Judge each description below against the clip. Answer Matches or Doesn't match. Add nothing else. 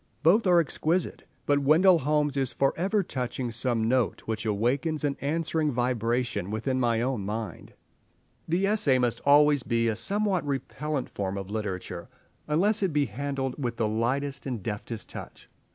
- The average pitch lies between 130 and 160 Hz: Matches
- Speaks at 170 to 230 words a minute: Doesn't match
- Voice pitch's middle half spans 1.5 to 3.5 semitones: Doesn't match